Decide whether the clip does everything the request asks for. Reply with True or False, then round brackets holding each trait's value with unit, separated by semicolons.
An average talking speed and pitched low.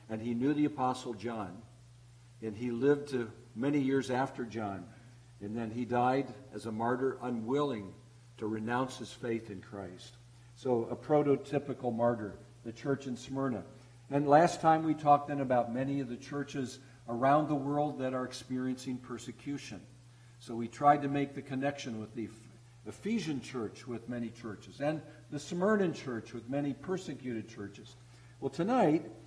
True (160 wpm; 125 Hz)